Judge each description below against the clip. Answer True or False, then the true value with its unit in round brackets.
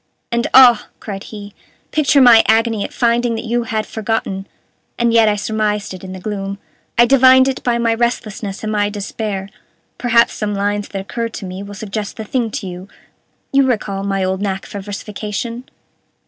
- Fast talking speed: False (185 wpm)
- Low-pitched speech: False (215 Hz)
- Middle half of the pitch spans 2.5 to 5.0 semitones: True (2.8 semitones)